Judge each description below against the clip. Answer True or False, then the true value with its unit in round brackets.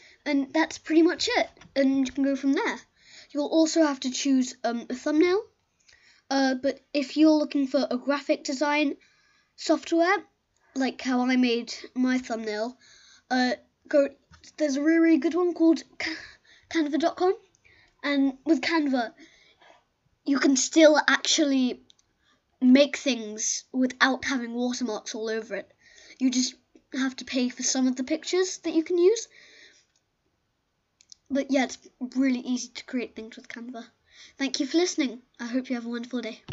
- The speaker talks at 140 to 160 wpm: True (155 wpm)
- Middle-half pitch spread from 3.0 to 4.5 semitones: True (4.2 semitones)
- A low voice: False (275 Hz)